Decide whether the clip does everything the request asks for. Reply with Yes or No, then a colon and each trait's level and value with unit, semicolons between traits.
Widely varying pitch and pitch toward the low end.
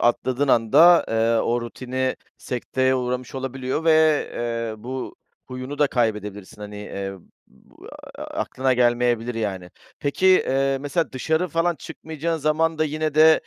No: average, 4.7 semitones; low, 130 Hz